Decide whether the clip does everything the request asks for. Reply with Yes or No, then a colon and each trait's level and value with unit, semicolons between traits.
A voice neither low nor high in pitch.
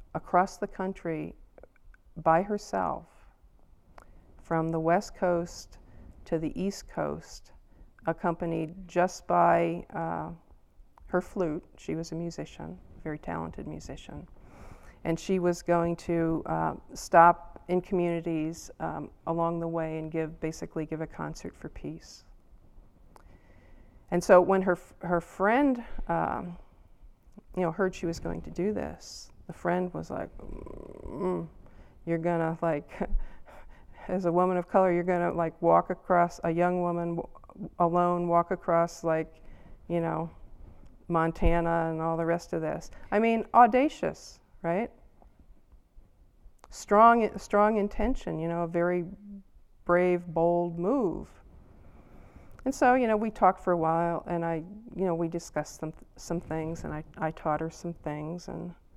Yes: medium, 170 Hz